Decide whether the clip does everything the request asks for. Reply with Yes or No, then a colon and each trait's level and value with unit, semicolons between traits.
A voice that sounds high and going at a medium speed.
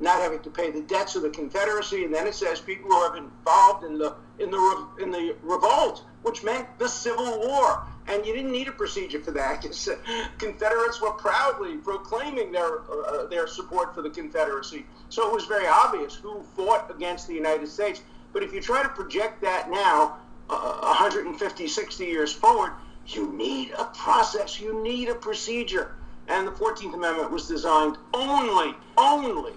Yes: high, 225 Hz; average, 180 wpm